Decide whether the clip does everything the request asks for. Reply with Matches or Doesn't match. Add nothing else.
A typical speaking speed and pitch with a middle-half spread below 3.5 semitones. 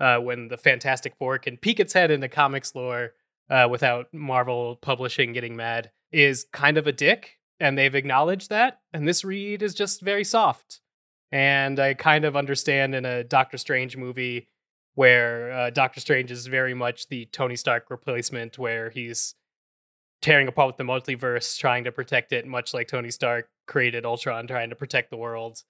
Matches